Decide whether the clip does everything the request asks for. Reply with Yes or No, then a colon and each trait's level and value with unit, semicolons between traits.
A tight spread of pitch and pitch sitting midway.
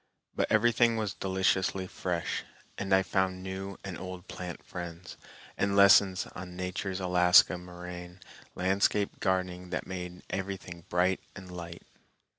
No: narrow, 1.4 semitones; very low, 95 Hz